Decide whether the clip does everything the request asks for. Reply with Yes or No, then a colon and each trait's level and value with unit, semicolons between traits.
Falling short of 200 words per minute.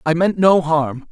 No: fast, 215 wpm